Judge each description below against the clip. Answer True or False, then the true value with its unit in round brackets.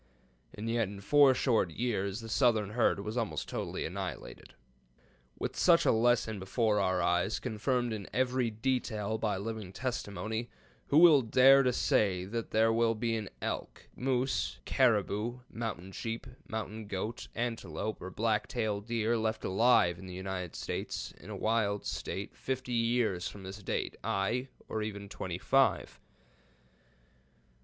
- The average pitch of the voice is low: True (110 Hz)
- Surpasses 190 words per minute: False (150 wpm)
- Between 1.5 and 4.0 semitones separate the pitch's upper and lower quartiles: True (3.1 semitones)